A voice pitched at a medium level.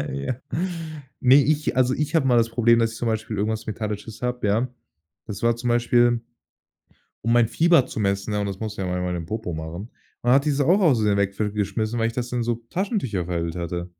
No: low, 115 Hz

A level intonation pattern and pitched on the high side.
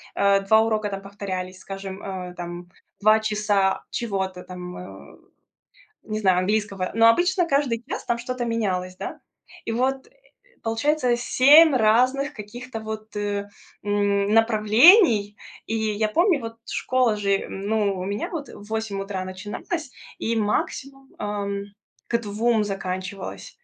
No: average, 3.1 semitones; high, 210 Hz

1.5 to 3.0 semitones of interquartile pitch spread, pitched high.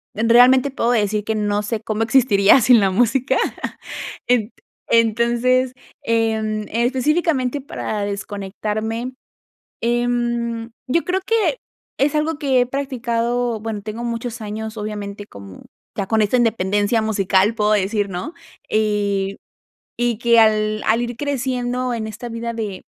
Yes: narrow, 2.6 semitones; high, 230 Hz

